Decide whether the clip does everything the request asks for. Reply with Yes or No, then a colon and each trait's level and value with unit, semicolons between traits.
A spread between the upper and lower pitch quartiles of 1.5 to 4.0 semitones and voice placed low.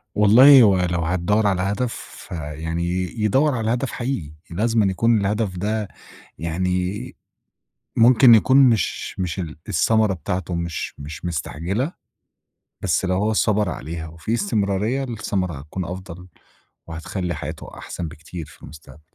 No: average, 4.6 semitones; very low, 95 Hz